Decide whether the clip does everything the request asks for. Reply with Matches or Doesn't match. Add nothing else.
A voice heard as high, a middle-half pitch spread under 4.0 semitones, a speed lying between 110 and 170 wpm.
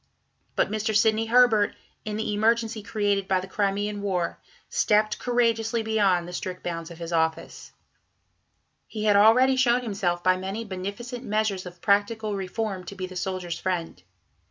Matches